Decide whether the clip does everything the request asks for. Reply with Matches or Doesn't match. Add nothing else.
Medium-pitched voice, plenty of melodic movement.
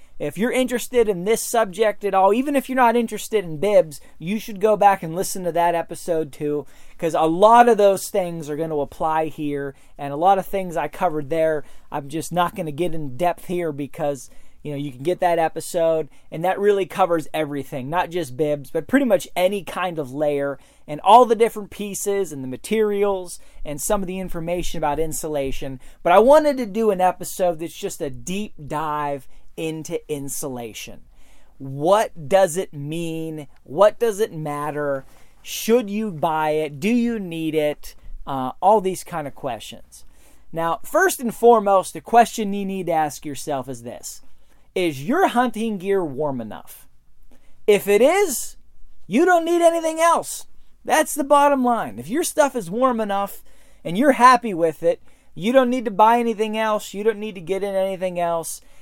Matches